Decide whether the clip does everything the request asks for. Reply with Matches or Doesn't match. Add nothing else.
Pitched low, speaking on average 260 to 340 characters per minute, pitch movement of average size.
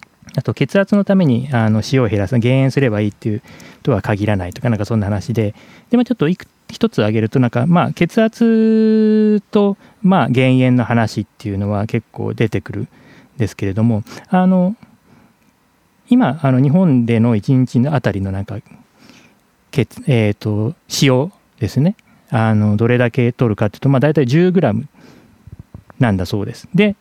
Doesn't match